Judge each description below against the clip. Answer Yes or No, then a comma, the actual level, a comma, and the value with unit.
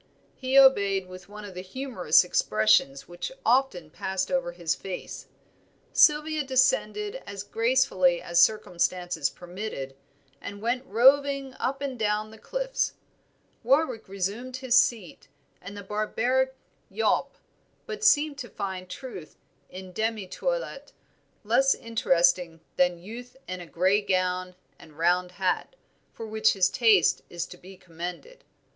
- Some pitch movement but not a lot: No, wide, 6.2 semitones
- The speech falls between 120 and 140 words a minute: Yes, slow, 135 wpm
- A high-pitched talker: Yes, high, 205 Hz